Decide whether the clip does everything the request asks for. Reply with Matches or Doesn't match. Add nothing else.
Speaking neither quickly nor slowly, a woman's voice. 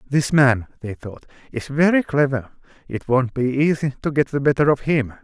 Doesn't match